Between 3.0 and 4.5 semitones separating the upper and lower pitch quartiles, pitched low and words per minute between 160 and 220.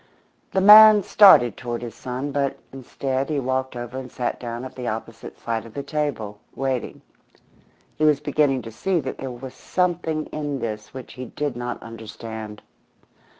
Yes: average, 3.7 semitones; low, 130 Hz; average, 170 wpm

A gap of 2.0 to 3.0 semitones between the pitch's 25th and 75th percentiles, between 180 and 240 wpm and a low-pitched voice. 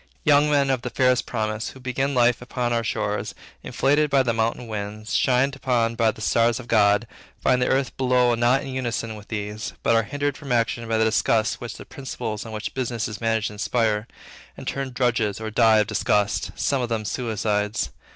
Yes: average, 2.7 semitones; fast, 205 wpm; low, 115 Hz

